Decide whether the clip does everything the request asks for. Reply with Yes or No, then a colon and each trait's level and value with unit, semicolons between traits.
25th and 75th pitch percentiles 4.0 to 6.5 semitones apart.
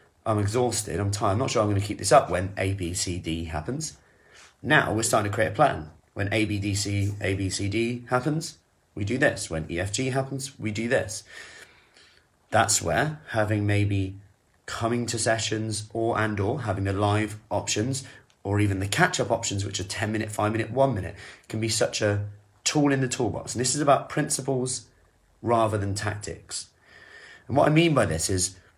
No: average, 3.3 semitones